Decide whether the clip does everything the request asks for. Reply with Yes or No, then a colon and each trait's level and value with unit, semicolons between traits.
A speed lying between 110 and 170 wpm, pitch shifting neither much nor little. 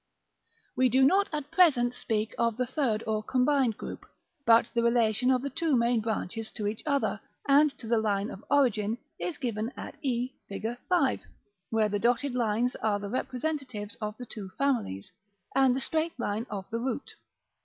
No: average, 180 wpm; average, 3.6 semitones